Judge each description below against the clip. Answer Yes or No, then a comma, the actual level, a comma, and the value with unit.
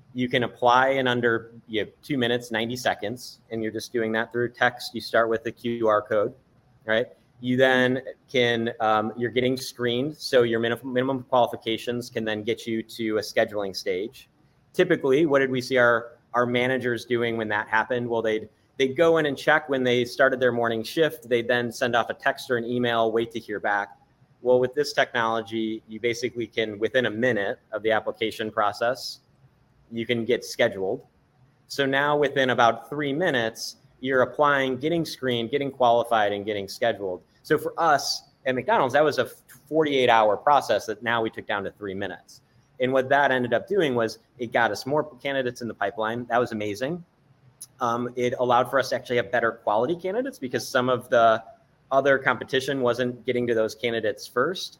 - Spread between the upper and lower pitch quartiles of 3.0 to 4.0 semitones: No, narrow, 2.5 semitones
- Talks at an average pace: Yes, average, 190 wpm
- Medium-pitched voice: No, low, 120 Hz